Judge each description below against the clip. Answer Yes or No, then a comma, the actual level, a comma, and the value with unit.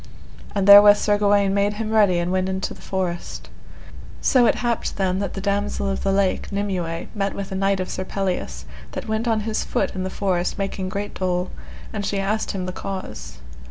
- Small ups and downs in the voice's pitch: Yes, narrow, 1.6 semitones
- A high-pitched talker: Yes, high, 195 Hz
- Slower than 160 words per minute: No, fast, 205 wpm